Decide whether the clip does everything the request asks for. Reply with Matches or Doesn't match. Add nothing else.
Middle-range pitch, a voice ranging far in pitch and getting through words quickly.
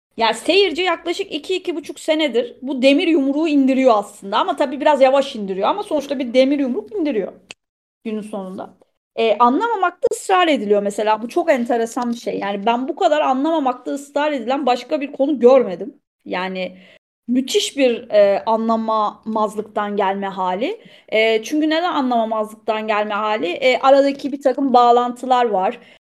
Doesn't match